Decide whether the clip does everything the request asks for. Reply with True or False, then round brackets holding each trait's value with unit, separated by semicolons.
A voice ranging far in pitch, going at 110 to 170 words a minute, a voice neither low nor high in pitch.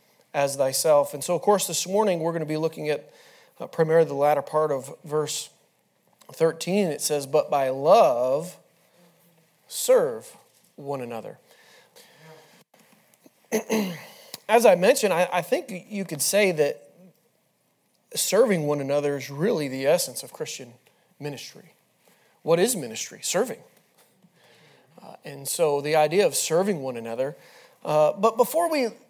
True (5.7 semitones; 140 wpm; 165 Hz)